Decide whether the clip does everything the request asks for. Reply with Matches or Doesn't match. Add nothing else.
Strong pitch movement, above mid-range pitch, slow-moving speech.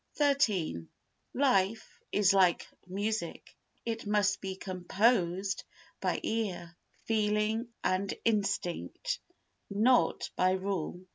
Doesn't match